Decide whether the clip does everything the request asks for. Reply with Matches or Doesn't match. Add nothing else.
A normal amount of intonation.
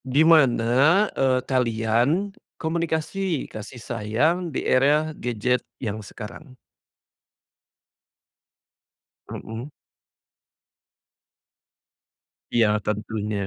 Doesn't match